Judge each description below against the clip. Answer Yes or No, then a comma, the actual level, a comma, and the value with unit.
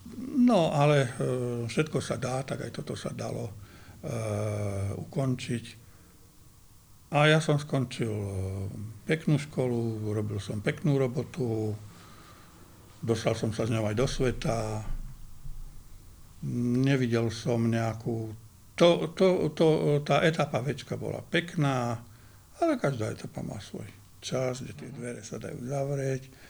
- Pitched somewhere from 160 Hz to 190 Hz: No, low, 120 Hz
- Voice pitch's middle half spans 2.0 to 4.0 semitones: No, average, 4.5 semitones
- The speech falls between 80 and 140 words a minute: Yes, average, 120 wpm